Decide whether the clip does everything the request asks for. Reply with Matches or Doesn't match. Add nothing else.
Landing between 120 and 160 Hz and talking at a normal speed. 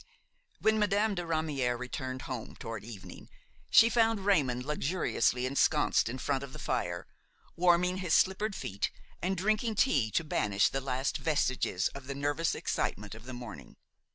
Matches